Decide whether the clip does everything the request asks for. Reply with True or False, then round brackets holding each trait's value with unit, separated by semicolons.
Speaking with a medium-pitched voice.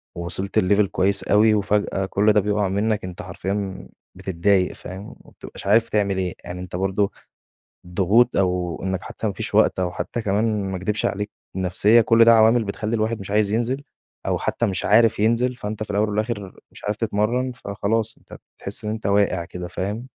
False (105 Hz)